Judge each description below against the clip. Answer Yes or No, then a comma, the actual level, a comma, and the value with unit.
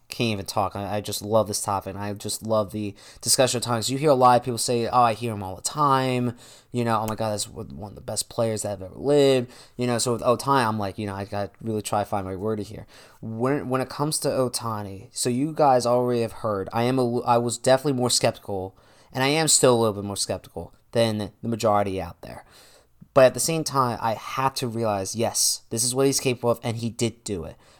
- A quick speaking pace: Yes, fast, 255 wpm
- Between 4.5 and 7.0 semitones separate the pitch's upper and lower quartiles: No, average, 3.2 semitones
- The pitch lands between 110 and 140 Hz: Yes, low, 115 Hz